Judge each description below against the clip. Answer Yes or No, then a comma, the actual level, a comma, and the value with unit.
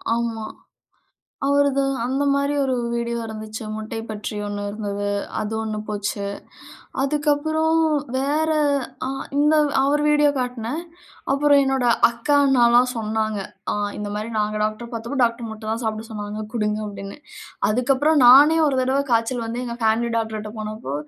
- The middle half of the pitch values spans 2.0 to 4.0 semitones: No, average, 4.4 semitones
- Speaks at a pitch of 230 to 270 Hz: Yes, high, 235 Hz